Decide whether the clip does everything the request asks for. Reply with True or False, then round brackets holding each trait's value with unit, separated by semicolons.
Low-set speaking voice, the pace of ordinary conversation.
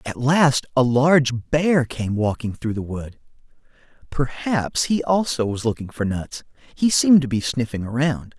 True (130 Hz; 165 wpm)